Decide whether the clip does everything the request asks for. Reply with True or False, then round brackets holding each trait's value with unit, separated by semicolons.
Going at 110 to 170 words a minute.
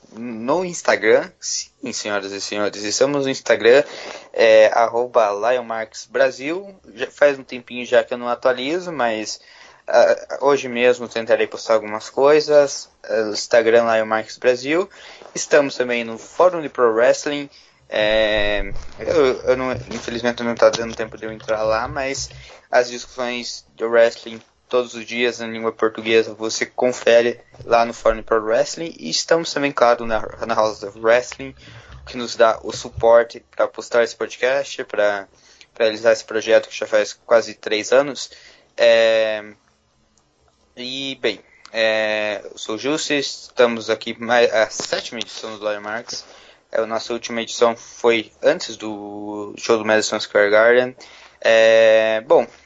True (145 wpm)